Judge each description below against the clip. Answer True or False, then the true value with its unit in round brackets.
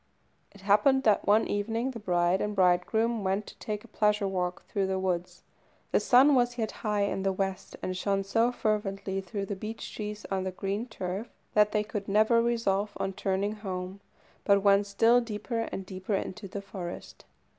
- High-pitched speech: True (200 Hz)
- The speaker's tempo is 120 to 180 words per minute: False (190 wpm)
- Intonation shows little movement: True (2.1 semitones)